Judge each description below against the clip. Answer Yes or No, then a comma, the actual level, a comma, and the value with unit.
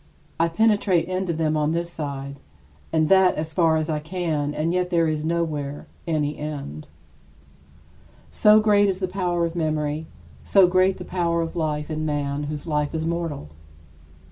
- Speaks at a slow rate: No, average, 170 wpm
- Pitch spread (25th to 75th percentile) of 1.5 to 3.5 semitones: Yes, average, 2.9 semitones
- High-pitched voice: No, medium, 160 Hz